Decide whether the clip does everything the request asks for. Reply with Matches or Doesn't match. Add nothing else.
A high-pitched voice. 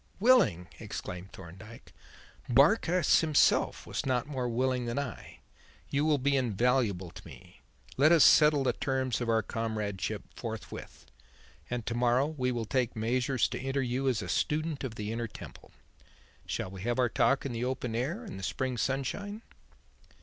Doesn't match